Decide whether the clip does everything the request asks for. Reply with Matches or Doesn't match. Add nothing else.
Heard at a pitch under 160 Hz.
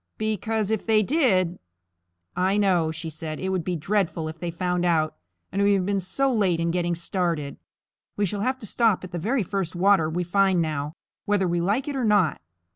Doesn't match